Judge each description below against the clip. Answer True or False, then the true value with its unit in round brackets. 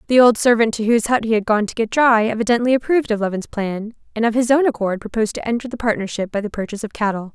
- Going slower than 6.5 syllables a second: False (7.1 syllables/s)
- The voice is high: True (225 Hz)